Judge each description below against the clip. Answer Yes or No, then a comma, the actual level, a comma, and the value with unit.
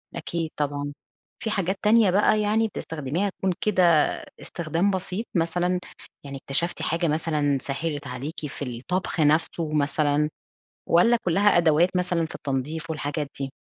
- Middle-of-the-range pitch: Yes, medium, 165 Hz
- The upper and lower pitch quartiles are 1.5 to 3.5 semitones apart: No, average, 3.9 semitones